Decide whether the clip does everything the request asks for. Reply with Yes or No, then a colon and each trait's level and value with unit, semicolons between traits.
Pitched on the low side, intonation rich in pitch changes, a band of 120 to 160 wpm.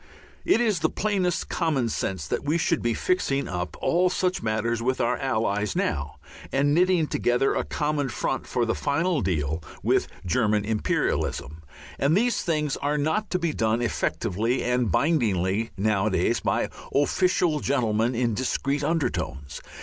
Yes: low, 130 Hz; wide, 6.8 semitones; average, 150 wpm